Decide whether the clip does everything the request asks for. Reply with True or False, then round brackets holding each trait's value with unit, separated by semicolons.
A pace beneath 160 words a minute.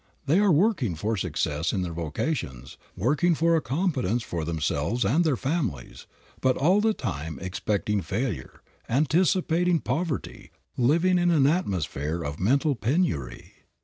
True (140 wpm)